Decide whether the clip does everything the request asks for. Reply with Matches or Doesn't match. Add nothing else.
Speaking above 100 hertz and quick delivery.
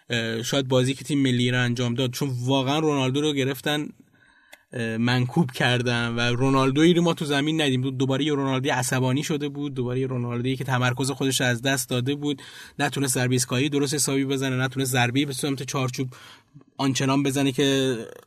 Matches